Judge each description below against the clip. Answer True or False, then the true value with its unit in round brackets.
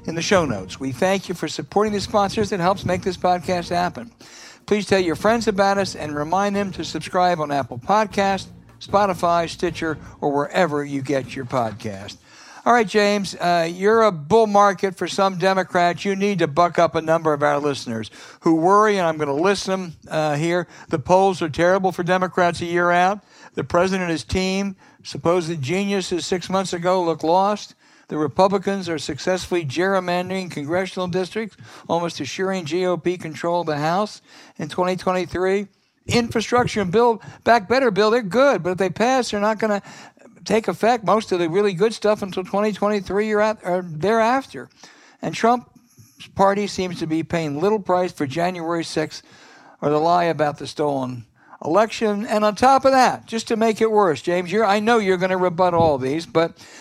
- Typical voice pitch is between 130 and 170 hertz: False (185 Hz)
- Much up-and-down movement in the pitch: False (3.7 semitones)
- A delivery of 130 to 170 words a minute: False (185 wpm)